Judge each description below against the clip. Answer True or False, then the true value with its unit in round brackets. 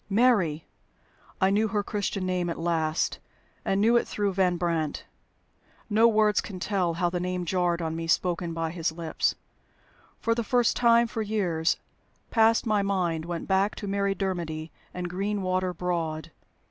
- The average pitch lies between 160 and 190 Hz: True (185 Hz)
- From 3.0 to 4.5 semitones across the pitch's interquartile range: True (3.5 semitones)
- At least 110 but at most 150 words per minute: False (160 wpm)